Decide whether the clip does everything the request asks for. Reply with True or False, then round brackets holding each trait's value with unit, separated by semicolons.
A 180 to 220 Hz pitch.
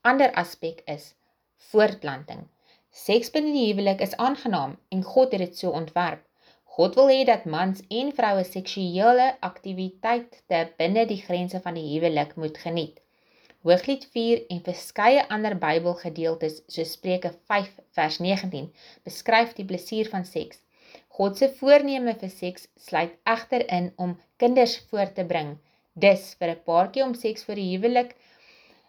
True (190 Hz)